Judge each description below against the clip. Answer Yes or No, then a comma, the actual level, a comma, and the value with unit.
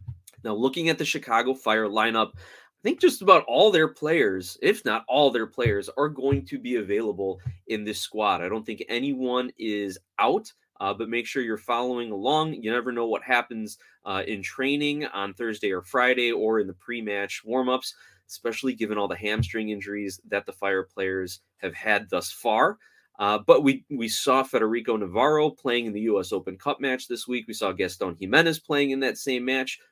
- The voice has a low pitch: Yes, low, 120 Hz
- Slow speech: No, average, 195 wpm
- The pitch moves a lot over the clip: No, average, 4.4 semitones